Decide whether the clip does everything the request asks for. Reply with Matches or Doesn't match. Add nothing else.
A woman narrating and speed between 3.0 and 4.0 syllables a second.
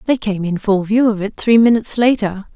Doesn't match